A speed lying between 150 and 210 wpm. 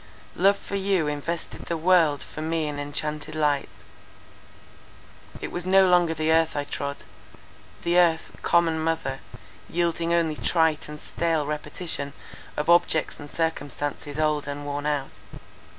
No: slow, 135 wpm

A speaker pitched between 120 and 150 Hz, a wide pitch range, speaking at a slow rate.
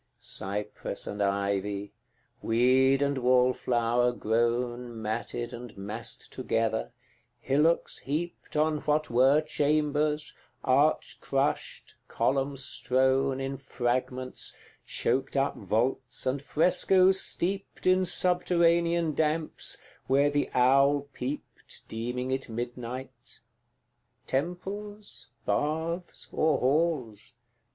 No: low, 135 Hz; average, 4.1 semitones; slow, 95 wpm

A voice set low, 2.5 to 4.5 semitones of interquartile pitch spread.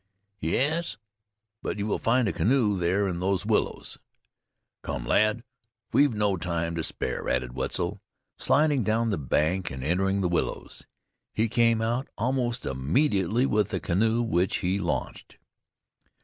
No: low, 100 Hz; average, 5.0 semitones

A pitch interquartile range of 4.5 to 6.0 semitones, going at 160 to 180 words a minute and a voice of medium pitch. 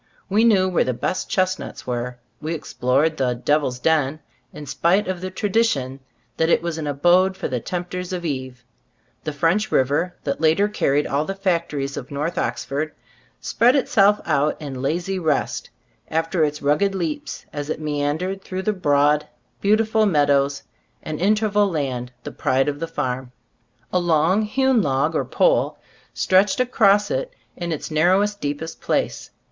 Yes: average, 5.1 semitones; average, 165 wpm; medium, 160 Hz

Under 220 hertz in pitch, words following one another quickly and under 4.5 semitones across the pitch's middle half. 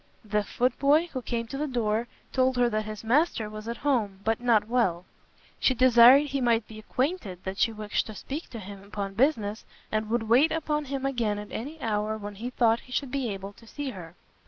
No: high, 230 Hz; fast, 220 wpm; average, 3.6 semitones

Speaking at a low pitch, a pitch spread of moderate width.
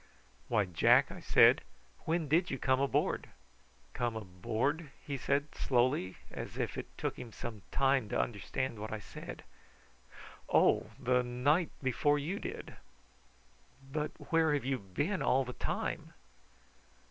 Yes: low, 130 Hz; average, 3.9 semitones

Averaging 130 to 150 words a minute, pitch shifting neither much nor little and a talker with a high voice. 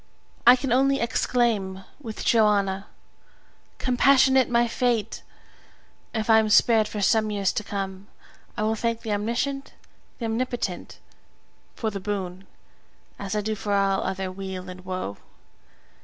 Yes: average, 140 wpm; average, 3.3 semitones; high, 215 Hz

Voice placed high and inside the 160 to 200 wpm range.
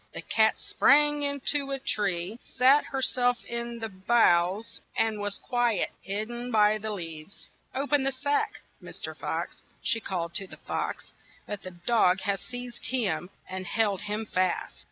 Yes: high, 220 Hz; average, 170 wpm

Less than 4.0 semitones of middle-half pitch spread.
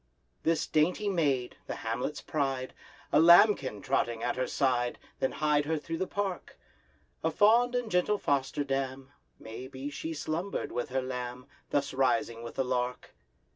No: average, 4.4 semitones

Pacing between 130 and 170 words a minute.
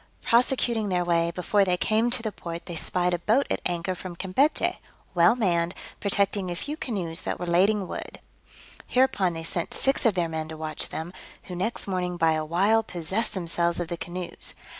No: average, 195 wpm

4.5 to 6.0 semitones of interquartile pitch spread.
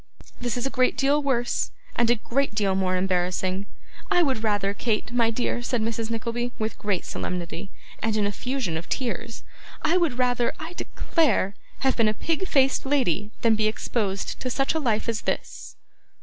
No: average, 4.1 semitones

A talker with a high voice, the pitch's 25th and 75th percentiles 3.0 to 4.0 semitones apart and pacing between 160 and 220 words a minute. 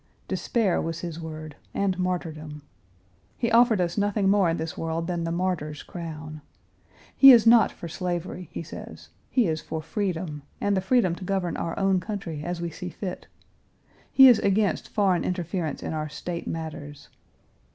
No: medium, 175 Hz; average, 3.5 semitones; average, 170 wpm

